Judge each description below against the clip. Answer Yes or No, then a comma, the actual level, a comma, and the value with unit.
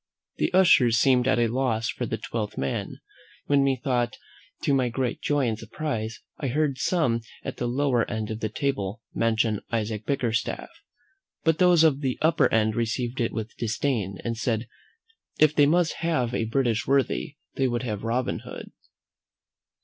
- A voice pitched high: No, low, 120 Hz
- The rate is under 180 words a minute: Yes, average, 165 wpm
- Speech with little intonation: No, average, 3.6 semitones